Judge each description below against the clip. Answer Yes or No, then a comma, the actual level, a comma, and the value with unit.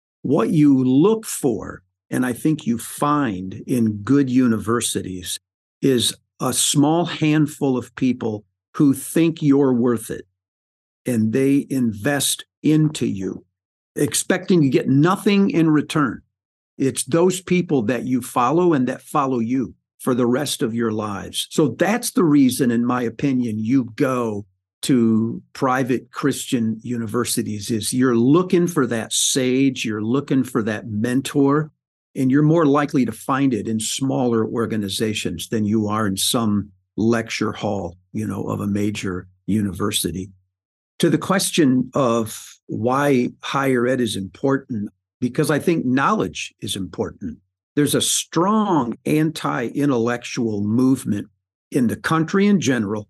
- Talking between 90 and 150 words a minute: Yes, average, 140 wpm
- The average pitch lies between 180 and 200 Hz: No, low, 125 Hz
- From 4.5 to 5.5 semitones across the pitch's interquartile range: Yes, average, 5.1 semitones